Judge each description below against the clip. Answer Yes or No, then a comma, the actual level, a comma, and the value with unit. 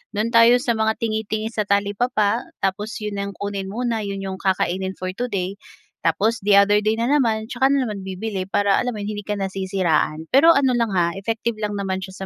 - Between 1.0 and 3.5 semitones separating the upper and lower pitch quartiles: Yes, average, 2.9 semitones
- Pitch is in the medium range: No, high, 205 Hz